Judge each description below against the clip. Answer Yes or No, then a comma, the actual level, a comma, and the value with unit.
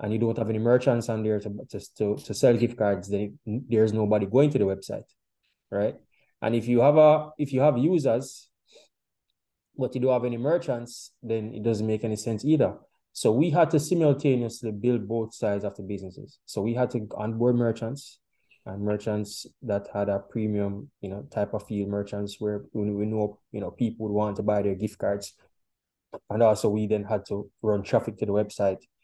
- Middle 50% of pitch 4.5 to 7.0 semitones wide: No, average, 2.7 semitones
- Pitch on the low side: Yes, low, 110 Hz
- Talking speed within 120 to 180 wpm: No, average, 200 wpm